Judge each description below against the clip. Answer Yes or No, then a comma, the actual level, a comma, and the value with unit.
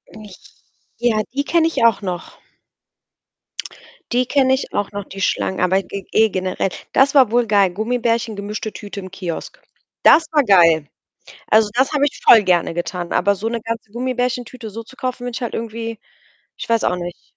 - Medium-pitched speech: No, high, 220 Hz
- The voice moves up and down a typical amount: Yes, average, 4.1 semitones